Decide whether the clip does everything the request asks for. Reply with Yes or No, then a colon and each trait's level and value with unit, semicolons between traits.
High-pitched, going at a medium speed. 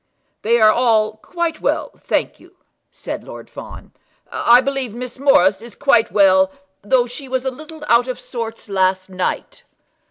Yes: high, 235 Hz; average, 160 wpm